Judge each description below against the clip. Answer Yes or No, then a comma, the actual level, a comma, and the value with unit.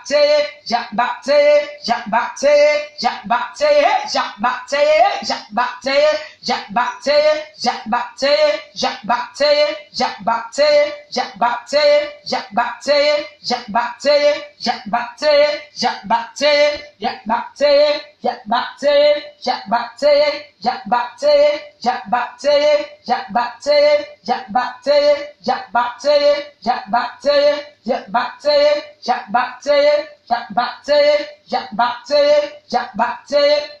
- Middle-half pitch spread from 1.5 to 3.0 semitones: No, average, 3.4 semitones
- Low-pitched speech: No, very high, 285 Hz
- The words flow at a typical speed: No, slow, 65 wpm